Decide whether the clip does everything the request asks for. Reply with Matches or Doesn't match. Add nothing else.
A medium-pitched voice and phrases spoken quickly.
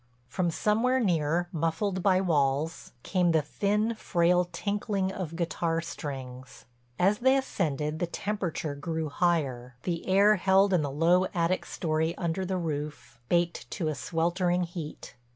Doesn't match